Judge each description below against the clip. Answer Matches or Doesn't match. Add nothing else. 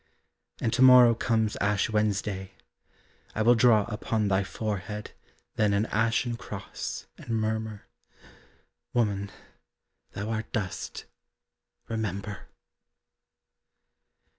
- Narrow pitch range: Matches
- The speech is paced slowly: Matches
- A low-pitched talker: Matches